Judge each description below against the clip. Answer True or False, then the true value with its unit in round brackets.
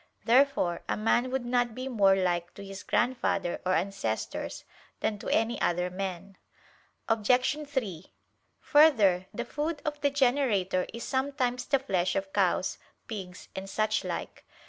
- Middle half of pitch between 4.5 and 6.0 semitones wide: True (5.4 semitones)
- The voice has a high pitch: True (220 Hz)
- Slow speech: False (145 wpm)